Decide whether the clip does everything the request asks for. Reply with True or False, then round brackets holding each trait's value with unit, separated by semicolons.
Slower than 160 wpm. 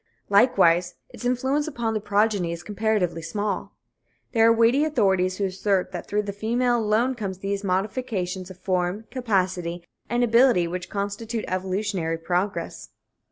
True (145 wpm)